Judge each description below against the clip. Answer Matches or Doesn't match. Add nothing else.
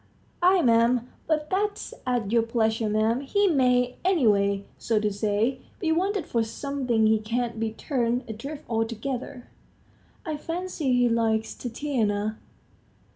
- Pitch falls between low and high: Doesn't match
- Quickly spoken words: Doesn't match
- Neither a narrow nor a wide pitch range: Matches